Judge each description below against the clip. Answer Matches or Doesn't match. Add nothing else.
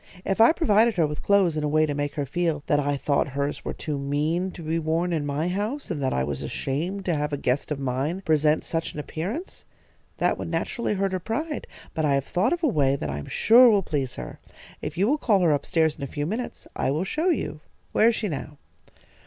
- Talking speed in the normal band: Doesn't match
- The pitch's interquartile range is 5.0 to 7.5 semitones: Matches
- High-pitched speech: Doesn't match